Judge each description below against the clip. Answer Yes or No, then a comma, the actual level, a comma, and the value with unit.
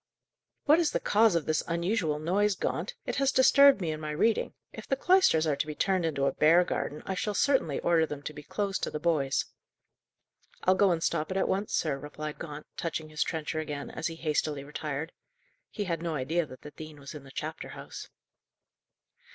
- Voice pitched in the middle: Yes, medium, 160 Hz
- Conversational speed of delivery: No, fast, 210 wpm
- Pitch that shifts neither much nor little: Yes, average, 4.1 semitones